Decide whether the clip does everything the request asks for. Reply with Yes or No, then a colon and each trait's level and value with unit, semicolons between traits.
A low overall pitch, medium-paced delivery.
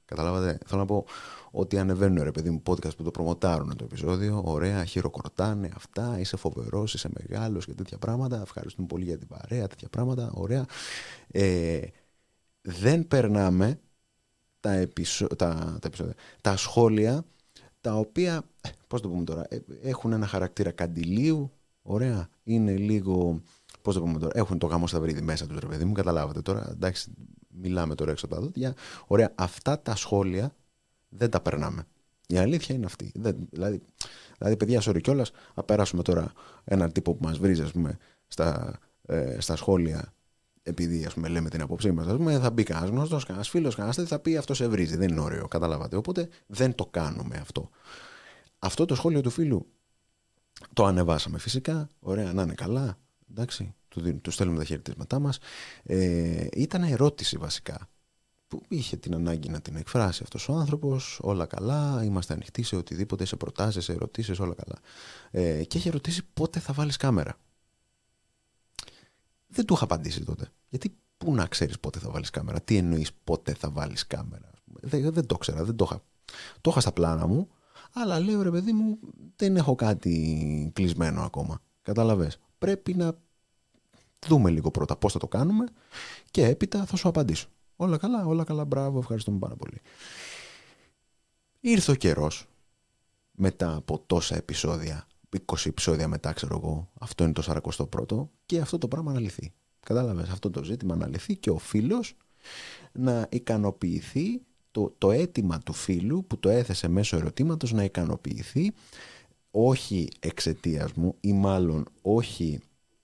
Yes: low, 100 Hz; average, 160 wpm